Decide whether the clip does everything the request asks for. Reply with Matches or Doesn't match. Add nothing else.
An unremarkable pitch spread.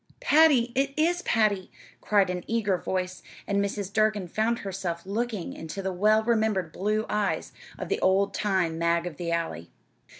Matches